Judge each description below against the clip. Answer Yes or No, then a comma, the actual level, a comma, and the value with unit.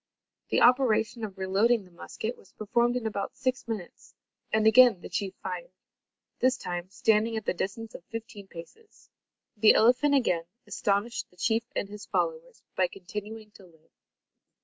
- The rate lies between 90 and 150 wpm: No, average, 160 wpm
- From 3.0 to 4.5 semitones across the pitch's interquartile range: Yes, average, 3.7 semitones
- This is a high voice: Yes, high, 215 Hz